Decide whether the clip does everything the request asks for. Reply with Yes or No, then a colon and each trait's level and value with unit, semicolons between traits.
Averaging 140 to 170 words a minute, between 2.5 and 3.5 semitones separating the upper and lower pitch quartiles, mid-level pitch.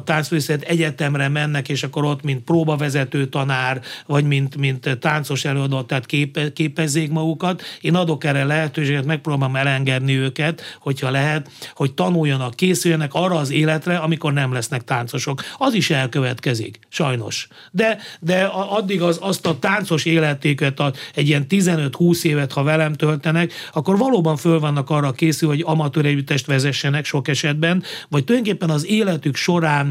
Yes: average, 150 wpm; average, 2.9 semitones; medium, 150 Hz